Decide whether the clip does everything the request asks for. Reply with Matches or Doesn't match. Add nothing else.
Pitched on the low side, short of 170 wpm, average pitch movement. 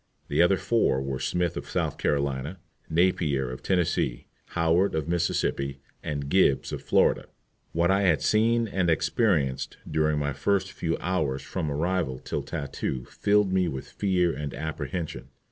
Matches